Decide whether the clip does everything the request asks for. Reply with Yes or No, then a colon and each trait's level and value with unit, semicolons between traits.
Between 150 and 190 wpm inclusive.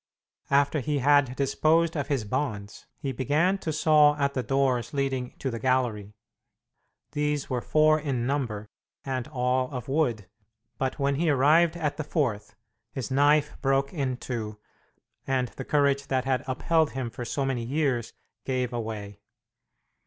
Yes: average, 155 wpm